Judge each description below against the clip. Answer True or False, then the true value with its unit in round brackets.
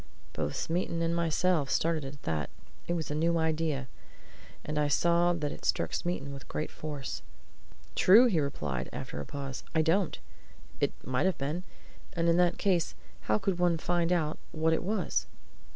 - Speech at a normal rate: True (175 wpm)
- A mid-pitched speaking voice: True (160 Hz)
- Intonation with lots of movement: False (3.3 semitones)